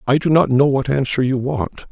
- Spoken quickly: Yes, fast, 250 wpm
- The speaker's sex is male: Yes, male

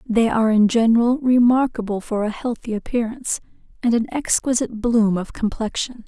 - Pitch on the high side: Yes, high, 230 Hz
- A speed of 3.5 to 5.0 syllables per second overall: No, 5.4 syllables/s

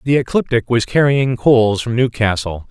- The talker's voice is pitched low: Yes, low, 120 Hz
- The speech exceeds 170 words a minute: No, average, 155 wpm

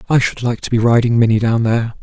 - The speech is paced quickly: Yes, fast, 265 wpm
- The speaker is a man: Yes, male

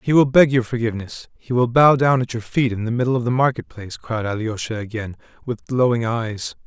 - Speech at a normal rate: No, fast, 225 wpm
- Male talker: Yes, male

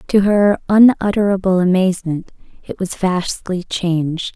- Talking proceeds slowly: Yes, slow, 110 wpm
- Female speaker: Yes, female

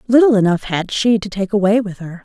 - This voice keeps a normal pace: No, fast, 240 wpm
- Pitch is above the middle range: Yes, high, 205 Hz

